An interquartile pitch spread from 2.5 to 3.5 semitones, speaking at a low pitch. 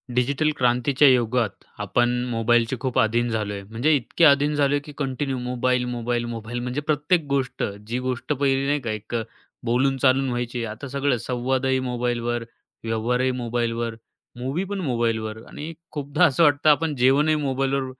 Yes: average, 3.0 semitones; low, 125 Hz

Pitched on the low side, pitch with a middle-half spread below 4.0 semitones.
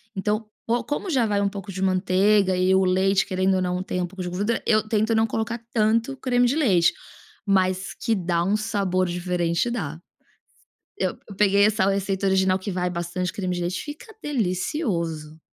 No: high, 190 Hz; average, 3.1 semitones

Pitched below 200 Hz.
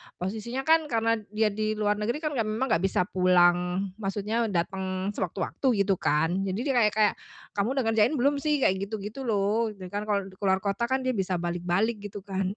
No: high, 205 Hz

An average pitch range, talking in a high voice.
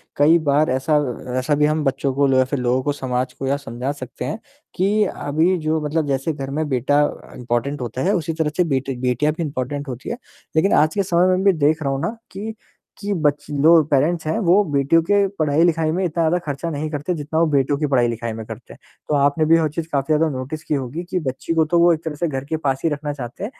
No: average, 3.4 semitones; medium, 150 Hz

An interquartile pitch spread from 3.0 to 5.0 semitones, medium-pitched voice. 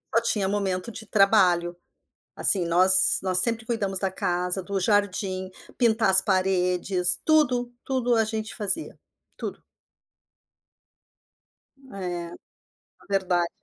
No: average, 3.3 semitones; high, 195 Hz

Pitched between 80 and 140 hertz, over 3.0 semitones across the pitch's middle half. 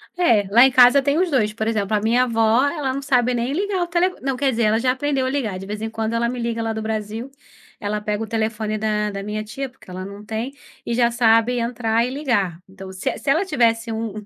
No: high, 230 Hz; average, 3.4 semitones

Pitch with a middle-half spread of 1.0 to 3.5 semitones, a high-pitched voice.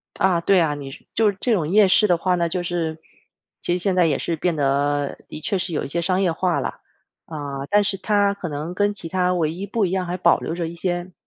No: average, 2.9 semitones; medium, 175 Hz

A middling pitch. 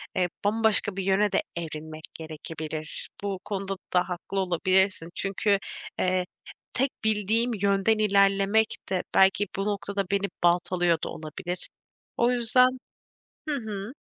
No: high, 195 Hz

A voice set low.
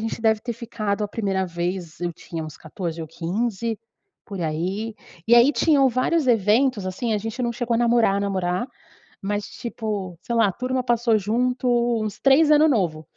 No: high, 215 Hz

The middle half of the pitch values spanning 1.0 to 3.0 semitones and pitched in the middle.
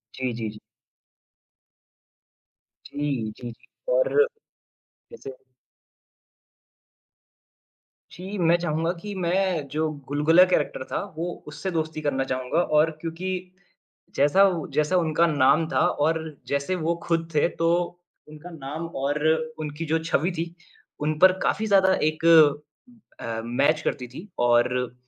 No: average, 3.4 semitones; medium, 155 Hz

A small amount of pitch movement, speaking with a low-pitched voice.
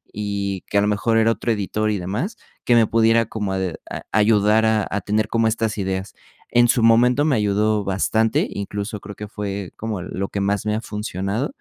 Yes: narrow, 2.0 semitones; low, 105 Hz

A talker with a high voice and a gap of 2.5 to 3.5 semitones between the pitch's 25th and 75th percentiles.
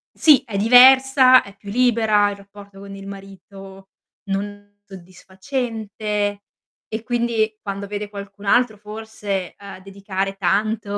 No: high, 205 Hz; narrow, 2.0 semitones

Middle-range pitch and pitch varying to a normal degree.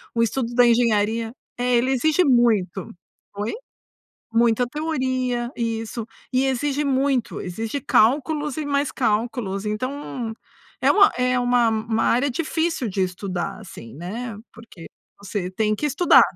No: high, 240 Hz; average, 3.6 semitones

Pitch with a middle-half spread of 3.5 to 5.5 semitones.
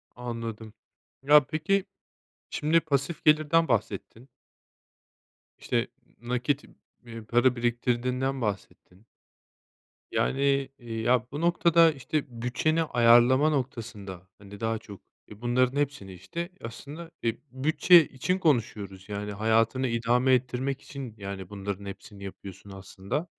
Yes: average, 4.8 semitones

